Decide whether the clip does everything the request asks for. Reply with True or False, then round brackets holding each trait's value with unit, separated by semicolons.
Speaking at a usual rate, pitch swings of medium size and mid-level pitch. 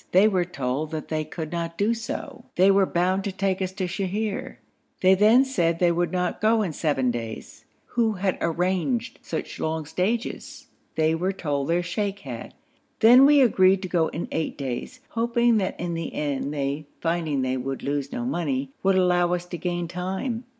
True (190 wpm; 4.2 semitones; 180 Hz)